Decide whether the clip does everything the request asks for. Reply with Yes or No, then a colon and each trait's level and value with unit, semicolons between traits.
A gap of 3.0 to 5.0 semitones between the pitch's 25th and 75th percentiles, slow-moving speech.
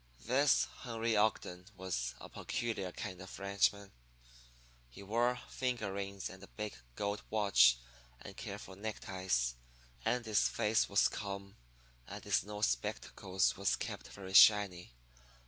No: narrow, 2.5 semitones; slow, 130 wpm